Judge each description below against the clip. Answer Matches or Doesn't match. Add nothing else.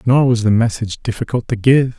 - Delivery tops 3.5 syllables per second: Matches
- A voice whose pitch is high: Doesn't match